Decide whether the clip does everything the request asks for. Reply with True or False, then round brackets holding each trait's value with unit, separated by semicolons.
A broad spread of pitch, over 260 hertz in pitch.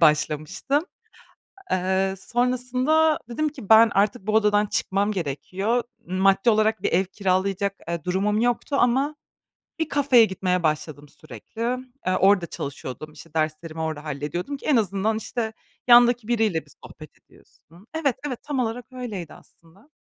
False (5.8 semitones; 205 Hz)